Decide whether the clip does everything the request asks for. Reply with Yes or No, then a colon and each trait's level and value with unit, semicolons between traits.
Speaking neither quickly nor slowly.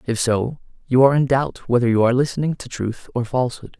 No: fast, 220 wpm